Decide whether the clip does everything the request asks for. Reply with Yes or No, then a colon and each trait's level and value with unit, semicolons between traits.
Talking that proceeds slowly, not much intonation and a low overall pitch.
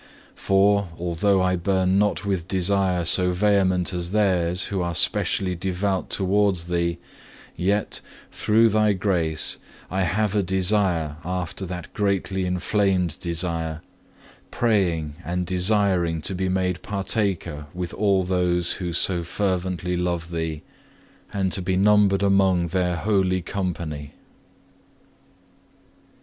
Yes: slow, 120 wpm; narrow, 2.2 semitones; very low, 90 Hz